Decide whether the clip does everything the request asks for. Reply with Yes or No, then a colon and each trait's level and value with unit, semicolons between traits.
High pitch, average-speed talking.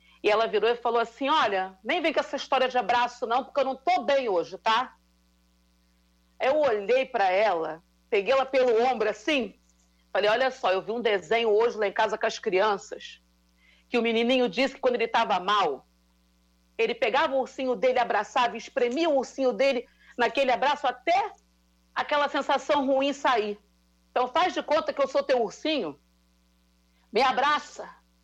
Yes: high, 235 Hz; average, 175 wpm